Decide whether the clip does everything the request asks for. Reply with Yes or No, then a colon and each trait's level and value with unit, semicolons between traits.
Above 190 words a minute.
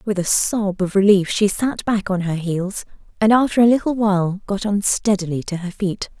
Yes: fast, 205 wpm